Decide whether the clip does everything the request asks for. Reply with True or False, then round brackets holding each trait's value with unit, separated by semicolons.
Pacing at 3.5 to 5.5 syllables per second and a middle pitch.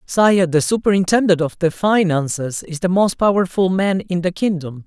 True (4.9 syllables/s; 180 Hz)